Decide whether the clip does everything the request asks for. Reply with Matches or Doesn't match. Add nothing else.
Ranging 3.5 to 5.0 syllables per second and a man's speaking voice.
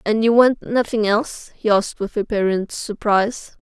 Doesn't match